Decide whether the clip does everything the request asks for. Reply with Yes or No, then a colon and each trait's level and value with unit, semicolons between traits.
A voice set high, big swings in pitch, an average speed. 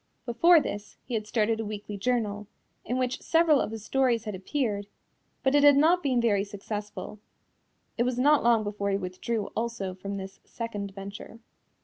No: high, 220 Hz; average, 3.7 semitones; average, 175 wpm